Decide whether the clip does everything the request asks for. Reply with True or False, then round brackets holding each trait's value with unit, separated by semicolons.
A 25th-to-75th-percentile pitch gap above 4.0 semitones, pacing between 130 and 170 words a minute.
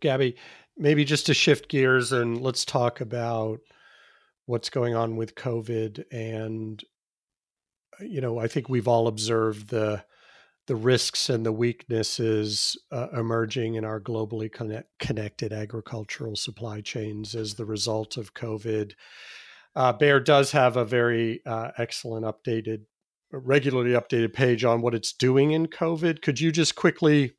False (3.3 semitones; 145 wpm)